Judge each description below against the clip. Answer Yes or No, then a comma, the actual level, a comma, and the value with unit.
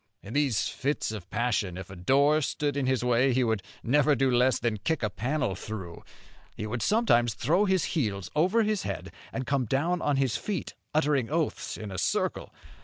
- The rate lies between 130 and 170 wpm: No, average, 195 wpm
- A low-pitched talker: Yes, low, 130 Hz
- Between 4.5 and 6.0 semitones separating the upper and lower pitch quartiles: Yes, wide, 5.4 semitones